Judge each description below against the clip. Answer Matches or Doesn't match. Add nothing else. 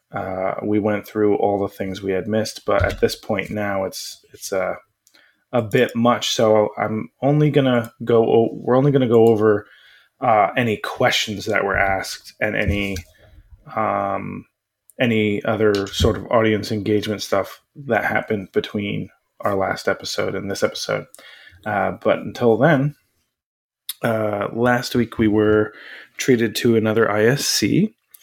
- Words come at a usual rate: Matches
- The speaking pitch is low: Matches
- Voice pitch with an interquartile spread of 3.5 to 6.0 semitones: Doesn't match